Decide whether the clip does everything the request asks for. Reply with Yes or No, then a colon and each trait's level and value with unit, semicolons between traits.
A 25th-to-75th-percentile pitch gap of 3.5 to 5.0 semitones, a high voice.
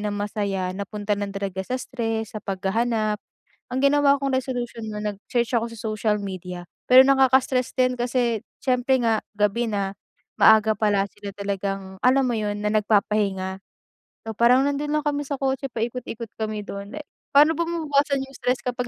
Yes: average, 4.2 semitones; high, 225 Hz